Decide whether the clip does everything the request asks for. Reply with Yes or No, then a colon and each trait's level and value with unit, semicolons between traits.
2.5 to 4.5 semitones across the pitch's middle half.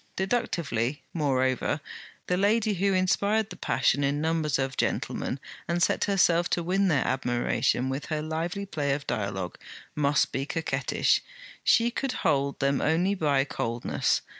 No: wide, 5.4 semitones